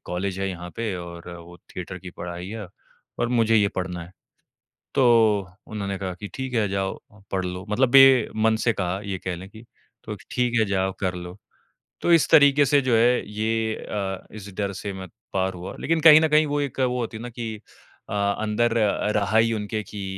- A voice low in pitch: Yes, low, 105 Hz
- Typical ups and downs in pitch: Yes, average, 4.1 semitones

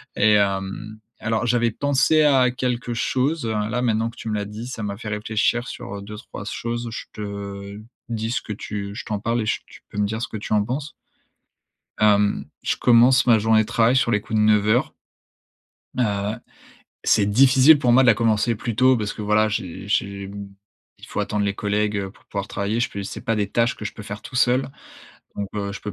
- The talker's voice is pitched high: No, low, 110 Hz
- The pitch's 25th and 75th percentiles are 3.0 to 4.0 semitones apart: No, narrow, 2.6 semitones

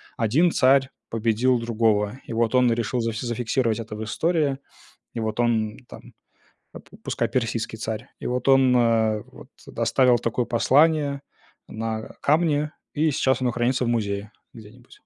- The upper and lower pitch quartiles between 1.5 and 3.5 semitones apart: Yes, average, 2.9 semitones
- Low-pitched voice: Yes, low, 120 Hz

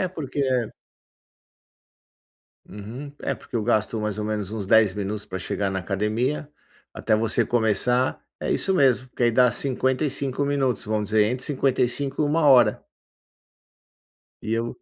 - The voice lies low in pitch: Yes, low, 120 Hz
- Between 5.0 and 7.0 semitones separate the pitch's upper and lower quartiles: No, average, 4.1 semitones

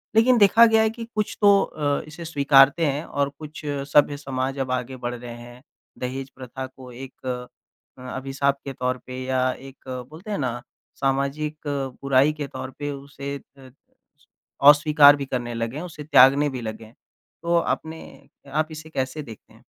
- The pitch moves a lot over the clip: No, average, 2.9 semitones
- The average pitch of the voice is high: No, medium, 140 Hz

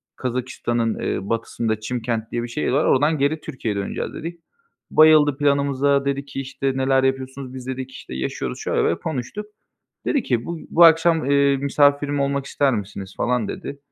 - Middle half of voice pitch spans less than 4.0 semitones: Yes, average, 2.7 semitones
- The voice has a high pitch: No, low, 135 Hz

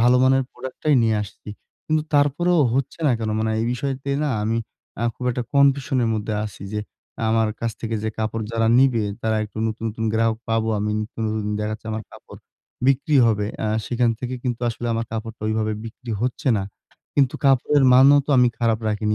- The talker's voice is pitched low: Yes, low, 115 Hz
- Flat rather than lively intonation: No, average, 3.2 semitones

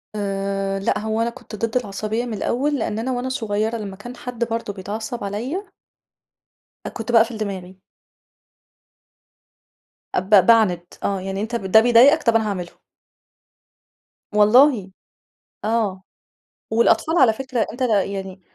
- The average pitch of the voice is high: Yes, high, 220 Hz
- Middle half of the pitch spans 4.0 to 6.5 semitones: No, average, 3.3 semitones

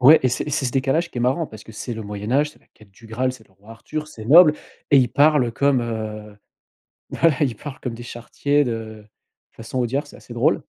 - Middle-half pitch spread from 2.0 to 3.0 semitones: No, average, 4.3 semitones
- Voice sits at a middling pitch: No, low, 125 Hz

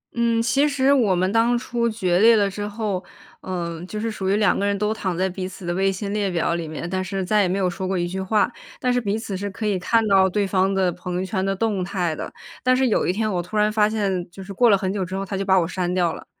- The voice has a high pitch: Yes, high, 195 Hz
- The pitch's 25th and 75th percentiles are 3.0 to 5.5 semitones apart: No, narrow, 2.6 semitones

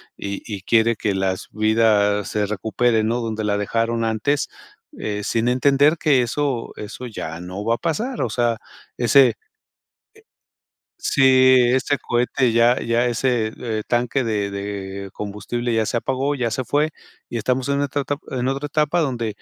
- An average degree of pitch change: Yes, average, 3.5 semitones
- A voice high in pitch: No, low, 115 Hz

